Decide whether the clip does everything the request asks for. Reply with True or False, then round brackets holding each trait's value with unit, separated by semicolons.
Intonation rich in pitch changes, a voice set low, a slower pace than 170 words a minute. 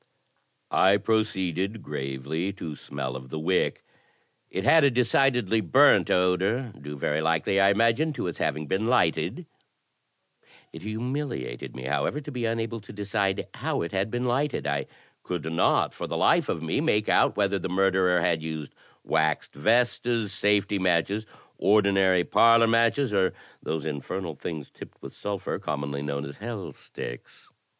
True (6.1 semitones; 95 Hz; 160 wpm)